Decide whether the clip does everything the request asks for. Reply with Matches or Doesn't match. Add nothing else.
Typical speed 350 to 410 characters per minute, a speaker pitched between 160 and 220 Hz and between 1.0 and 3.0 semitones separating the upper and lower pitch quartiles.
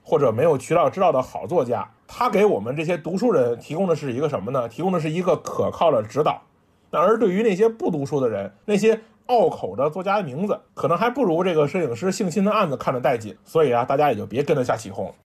Doesn't match